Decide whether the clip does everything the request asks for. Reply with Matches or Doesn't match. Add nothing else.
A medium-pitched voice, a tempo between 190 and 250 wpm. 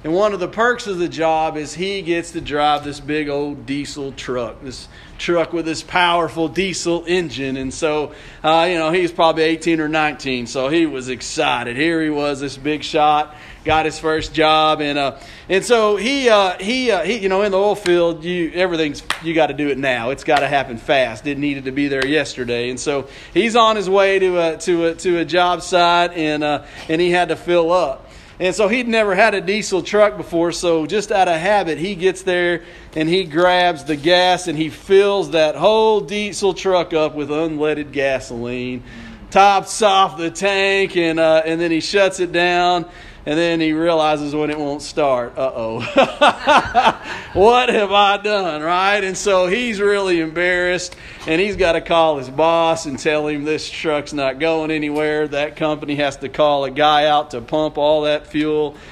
Matches